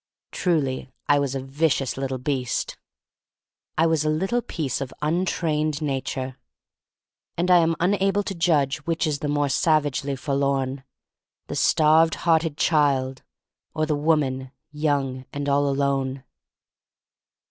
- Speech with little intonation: No, average, 3.0 semitones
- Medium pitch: Yes, medium, 145 Hz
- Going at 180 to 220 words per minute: No, slow, 135 wpm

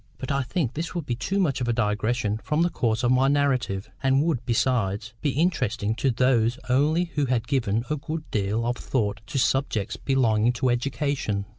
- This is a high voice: No, low, 125 Hz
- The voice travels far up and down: No, average, 4.1 semitones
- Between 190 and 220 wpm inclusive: Yes, average, 195 wpm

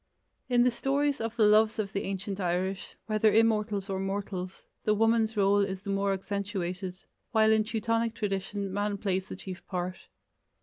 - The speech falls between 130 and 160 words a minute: No, average, 170 wpm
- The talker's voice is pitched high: Yes, high, 205 Hz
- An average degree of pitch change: No, narrow, 2.2 semitones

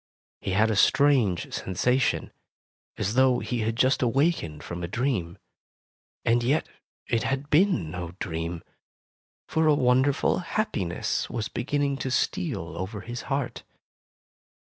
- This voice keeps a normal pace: No, slow, 130 wpm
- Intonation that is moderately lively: No, wide, 6.8 semitones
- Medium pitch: No, low, 120 Hz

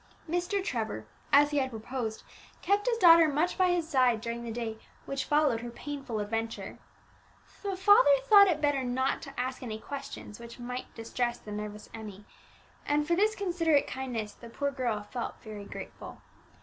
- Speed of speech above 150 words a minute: Yes, average, 175 wpm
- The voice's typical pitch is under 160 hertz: No, very high, 260 Hz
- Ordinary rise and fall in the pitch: No, wide, 6.1 semitones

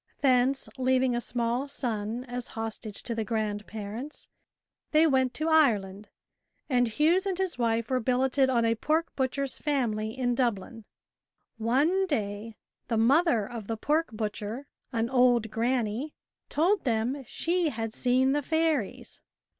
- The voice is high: Yes, high, 245 Hz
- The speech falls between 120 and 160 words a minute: Yes, average, 140 wpm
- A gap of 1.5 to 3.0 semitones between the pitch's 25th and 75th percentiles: No, average, 3.9 semitones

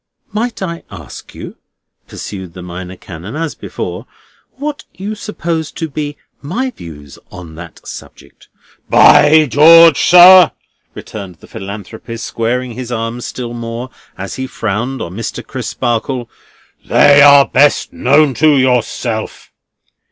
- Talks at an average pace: No, slow, 130 wpm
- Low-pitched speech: Yes, low, 125 Hz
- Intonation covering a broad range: Yes, wide, 6.4 semitones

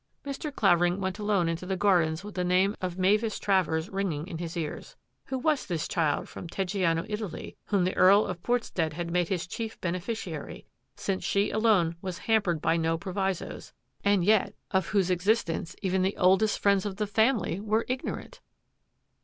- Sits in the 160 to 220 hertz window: Yes, high, 190 Hz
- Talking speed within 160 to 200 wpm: Yes, average, 180 wpm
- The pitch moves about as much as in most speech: Yes, average, 3.2 semitones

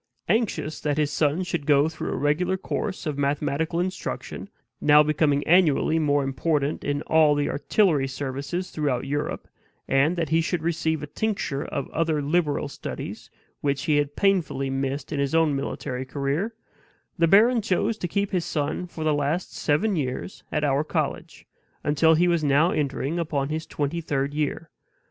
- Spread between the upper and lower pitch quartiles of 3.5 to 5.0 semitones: No, average, 3.0 semitones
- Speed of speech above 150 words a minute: Yes, average, 170 wpm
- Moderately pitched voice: Yes, medium, 150 Hz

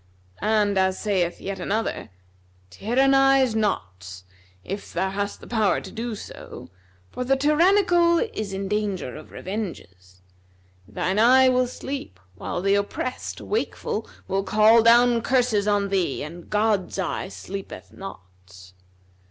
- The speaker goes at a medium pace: No, slow, 130 wpm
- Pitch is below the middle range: No, high, 205 Hz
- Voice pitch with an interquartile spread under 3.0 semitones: No, wide, 5.4 semitones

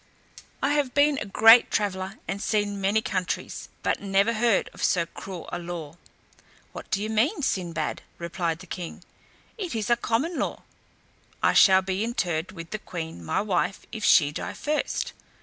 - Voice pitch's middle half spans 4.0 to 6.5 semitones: Yes, average, 4.3 semitones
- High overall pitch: Yes, high, 195 Hz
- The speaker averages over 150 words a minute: Yes, average, 170 wpm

